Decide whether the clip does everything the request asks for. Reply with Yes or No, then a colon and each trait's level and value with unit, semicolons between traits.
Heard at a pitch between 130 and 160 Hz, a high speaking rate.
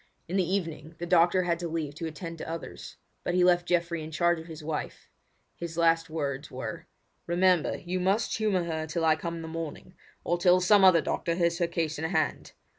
No: medium, 170 Hz; fast, 215 wpm